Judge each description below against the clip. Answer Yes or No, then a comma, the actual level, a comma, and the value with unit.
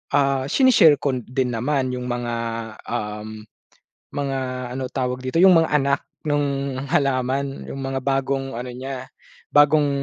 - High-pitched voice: No, low, 135 Hz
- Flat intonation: Yes, narrow, 1.9 semitones